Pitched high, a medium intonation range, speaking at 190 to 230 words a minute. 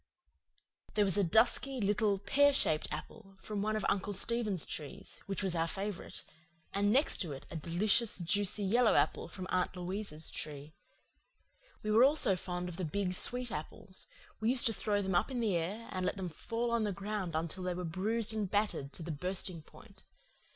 Yes: high, 195 Hz; average, 3.4 semitones; average, 195 wpm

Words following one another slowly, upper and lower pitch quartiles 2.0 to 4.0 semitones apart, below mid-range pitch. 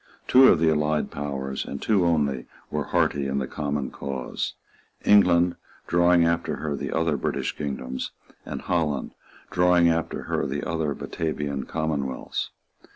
No: average, 145 wpm; average, 3.4 semitones; very low, 75 Hz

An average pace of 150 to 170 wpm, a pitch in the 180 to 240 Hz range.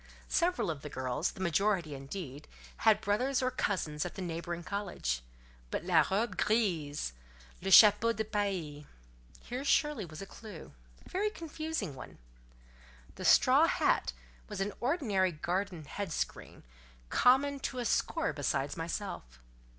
No: average, 140 wpm; high, 190 Hz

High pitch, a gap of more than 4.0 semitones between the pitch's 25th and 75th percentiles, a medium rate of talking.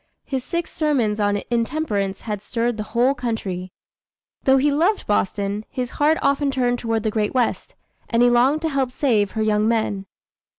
Yes: high, 235 Hz; average, 4.5 semitones; average, 175 wpm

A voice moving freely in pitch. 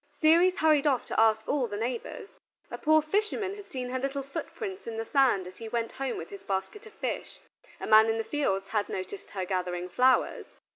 Yes: wide, 6.4 semitones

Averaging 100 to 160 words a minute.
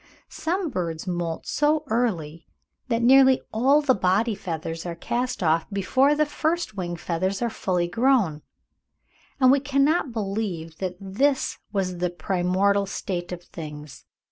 Yes: average, 140 wpm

